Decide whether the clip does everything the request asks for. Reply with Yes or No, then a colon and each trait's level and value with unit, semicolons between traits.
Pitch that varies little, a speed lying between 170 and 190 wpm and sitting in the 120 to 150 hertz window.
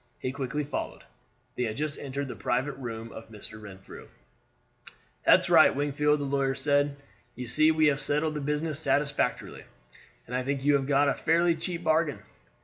Yes: narrow, 2.3 semitones; average, 175 wpm; medium, 140 Hz